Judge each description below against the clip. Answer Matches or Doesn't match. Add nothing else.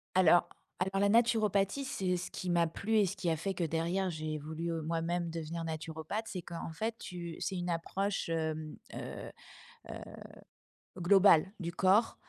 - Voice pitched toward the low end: Doesn't match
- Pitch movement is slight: Doesn't match